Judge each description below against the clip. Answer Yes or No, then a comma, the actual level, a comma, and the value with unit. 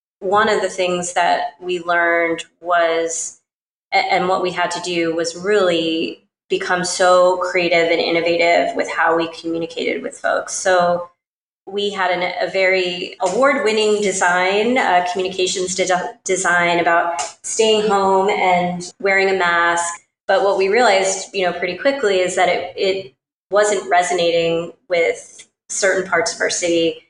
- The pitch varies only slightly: Yes, narrow, 2.1 semitones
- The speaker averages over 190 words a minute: No, average, 145 wpm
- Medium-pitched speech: Yes, medium, 180 Hz